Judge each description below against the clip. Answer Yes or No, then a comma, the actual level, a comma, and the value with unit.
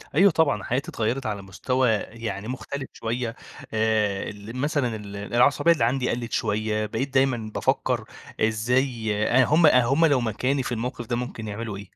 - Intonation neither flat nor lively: Yes, average, 3.3 semitones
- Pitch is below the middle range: Yes, low, 120 Hz